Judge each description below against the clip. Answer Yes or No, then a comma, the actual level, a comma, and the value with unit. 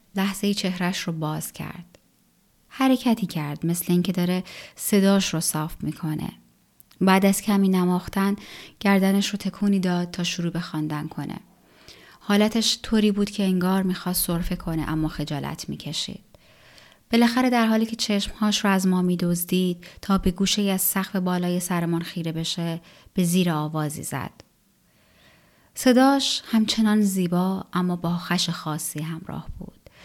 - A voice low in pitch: No, medium, 185 Hz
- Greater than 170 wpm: No, average, 140 wpm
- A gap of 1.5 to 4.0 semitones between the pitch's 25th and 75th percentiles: Yes, average, 2.9 semitones